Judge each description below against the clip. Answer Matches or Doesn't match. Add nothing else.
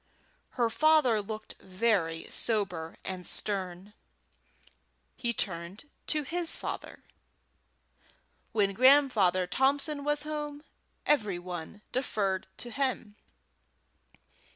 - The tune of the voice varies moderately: Doesn't match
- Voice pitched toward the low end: Doesn't match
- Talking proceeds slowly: Matches